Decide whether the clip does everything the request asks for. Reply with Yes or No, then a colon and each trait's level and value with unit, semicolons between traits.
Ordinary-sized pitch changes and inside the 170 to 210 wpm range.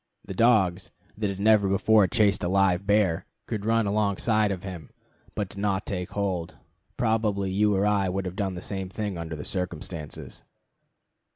No: narrow, 2.2 semitones; average, 175 wpm